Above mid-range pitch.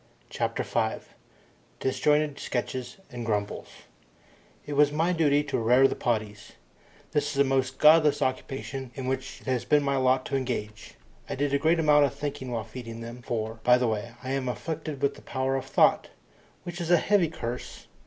No: low, 135 Hz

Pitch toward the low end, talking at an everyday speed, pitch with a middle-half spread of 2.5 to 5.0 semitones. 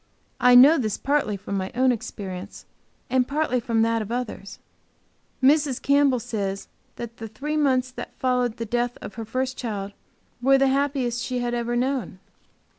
No: high, 245 Hz; average, 170 wpm; average, 3.0 semitones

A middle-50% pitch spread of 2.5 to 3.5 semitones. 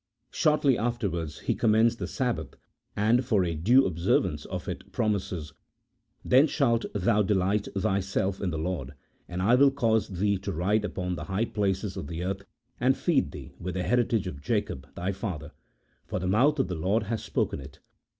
No: average, 4.2 semitones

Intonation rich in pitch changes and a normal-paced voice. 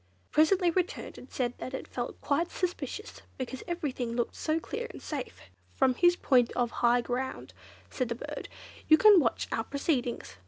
Yes: wide, 5.8 semitones; average, 180 wpm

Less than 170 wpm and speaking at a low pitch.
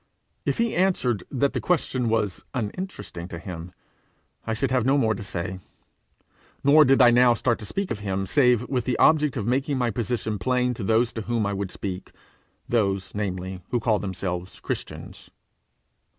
No: average, 180 wpm; low, 115 Hz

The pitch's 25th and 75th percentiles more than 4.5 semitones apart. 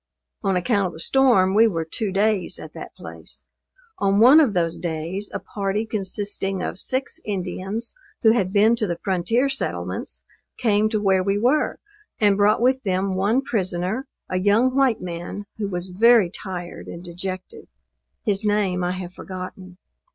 No: average, 3.1 semitones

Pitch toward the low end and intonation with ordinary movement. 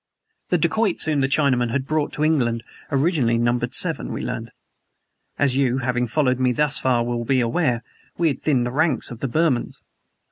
Yes: low, 130 Hz; average, 3.7 semitones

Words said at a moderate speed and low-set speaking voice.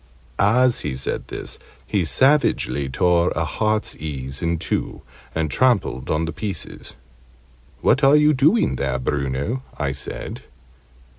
No: slow, 130 wpm; very low, 85 Hz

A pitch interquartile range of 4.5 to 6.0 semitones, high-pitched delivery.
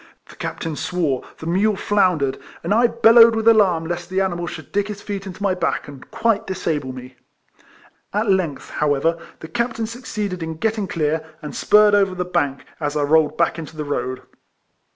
No: average, 5.2 semitones; medium, 180 Hz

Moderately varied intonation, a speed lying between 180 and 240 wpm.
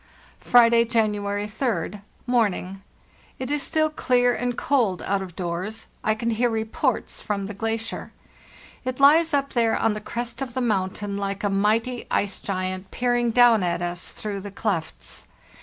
No: average, 3.5 semitones; average, 160 wpm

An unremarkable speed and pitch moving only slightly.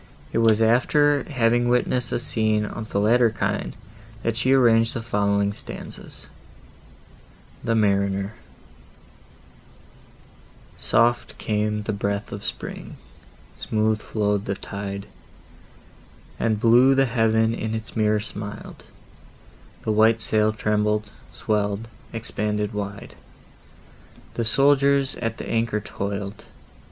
No: slow, 115 wpm; narrow, 2.0 semitones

